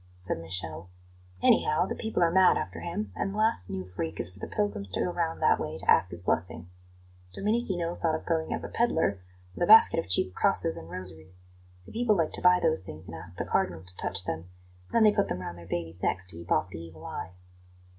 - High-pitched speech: No, very low, 95 Hz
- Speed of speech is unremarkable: No, fast, 235 wpm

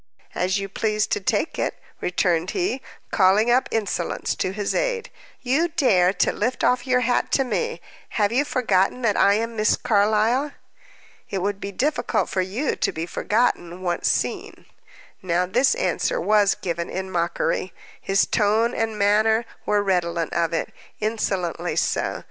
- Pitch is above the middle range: Yes, high, 210 Hz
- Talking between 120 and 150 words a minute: No, average, 160 wpm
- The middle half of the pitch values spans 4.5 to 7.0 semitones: Yes, average, 4.8 semitones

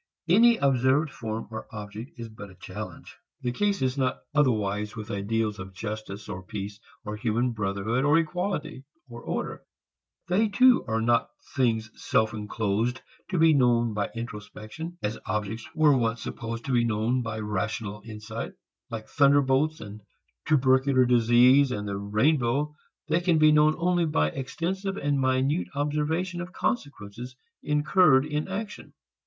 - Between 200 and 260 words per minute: No, average, 150 wpm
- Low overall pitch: Yes, low, 125 Hz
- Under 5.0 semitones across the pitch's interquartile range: No, wide, 5.6 semitones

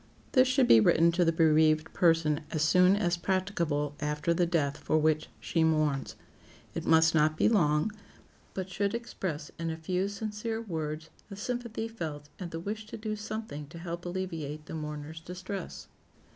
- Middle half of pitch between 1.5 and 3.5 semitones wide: No, average, 4.2 semitones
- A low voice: No, medium, 165 Hz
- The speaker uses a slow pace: No, average, 170 wpm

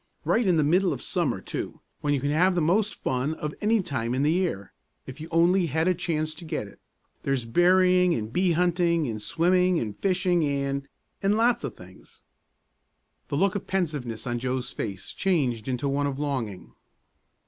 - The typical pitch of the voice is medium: Yes, medium, 155 Hz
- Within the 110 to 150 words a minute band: No, average, 190 wpm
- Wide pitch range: Yes, wide, 5.7 semitones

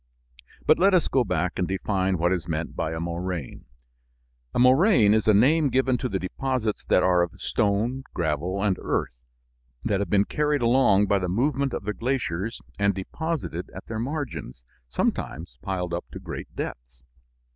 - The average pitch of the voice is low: Yes, low, 100 Hz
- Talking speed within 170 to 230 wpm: Yes, average, 175 wpm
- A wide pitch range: Yes, wide, 6.5 semitones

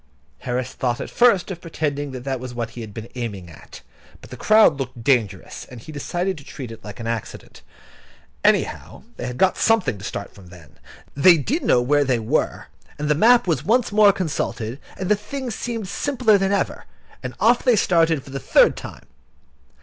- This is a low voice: No, medium, 145 Hz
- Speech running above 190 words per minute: Yes, average, 200 wpm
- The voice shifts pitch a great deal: Yes, wide, 8.4 semitones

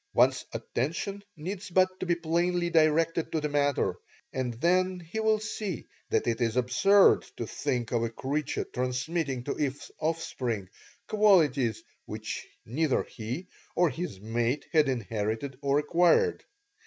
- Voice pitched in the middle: Yes, medium, 150 Hz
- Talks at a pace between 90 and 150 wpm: Yes, average, 140 wpm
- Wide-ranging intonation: Yes, wide, 5.9 semitones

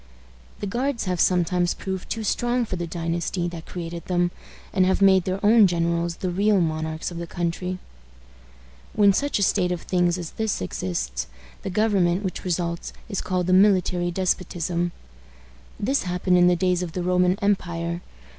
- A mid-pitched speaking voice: Yes, medium, 180 Hz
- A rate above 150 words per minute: Yes, average, 170 wpm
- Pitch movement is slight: Yes, narrow, 2.0 semitones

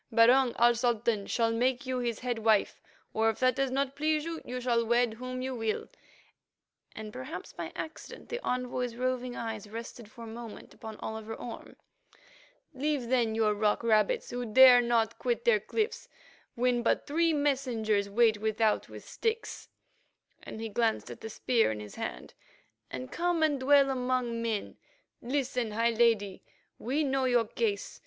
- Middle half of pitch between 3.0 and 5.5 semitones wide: No, narrow, 2.6 semitones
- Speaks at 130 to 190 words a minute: Yes, average, 165 wpm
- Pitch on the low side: No, high, 235 Hz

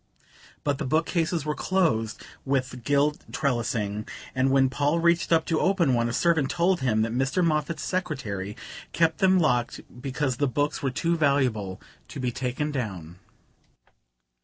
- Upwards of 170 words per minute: No, average, 155 wpm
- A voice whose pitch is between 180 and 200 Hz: No, medium, 140 Hz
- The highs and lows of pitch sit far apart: No, average, 4.9 semitones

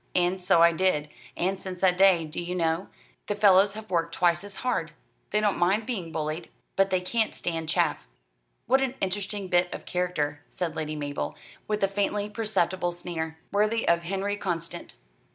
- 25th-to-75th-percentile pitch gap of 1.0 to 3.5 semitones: Yes, average, 3.2 semitones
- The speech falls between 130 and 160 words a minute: No, average, 180 wpm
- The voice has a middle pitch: Yes, medium, 180 Hz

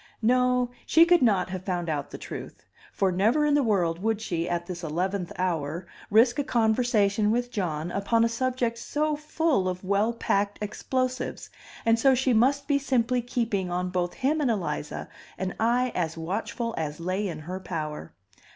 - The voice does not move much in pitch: No, wide, 5.6 semitones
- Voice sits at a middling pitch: No, high, 210 Hz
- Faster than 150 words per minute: Yes, average, 180 wpm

